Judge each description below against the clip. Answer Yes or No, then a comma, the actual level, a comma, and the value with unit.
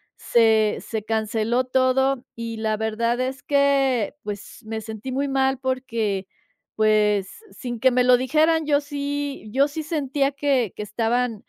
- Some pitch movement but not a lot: Yes, average, 3.7 semitones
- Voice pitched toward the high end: Yes, very high, 250 Hz